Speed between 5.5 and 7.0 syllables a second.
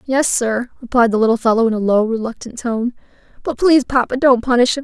Yes: 6.0 syllables/s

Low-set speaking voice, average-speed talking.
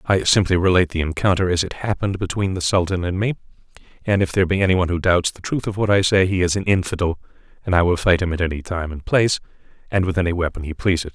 No: very low, 90 Hz; fast, 255 wpm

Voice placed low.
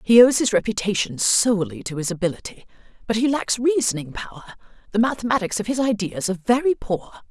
No: high, 215 Hz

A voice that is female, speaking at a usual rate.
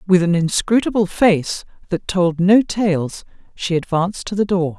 Yes: female; average, 165 wpm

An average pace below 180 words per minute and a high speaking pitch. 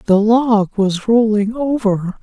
Yes: slow, 135 wpm; high, 215 Hz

